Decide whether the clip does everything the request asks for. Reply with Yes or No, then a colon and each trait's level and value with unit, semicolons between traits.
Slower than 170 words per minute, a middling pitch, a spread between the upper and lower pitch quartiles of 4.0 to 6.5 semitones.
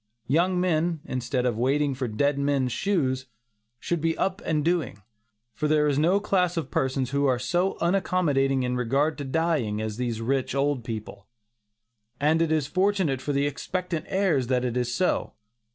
No: average, 175 wpm; medium, 145 Hz; average, 4.8 semitones